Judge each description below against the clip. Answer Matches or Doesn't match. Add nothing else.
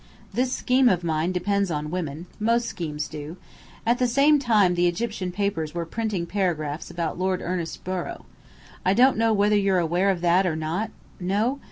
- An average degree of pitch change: Matches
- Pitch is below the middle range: Doesn't match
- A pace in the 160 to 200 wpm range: Matches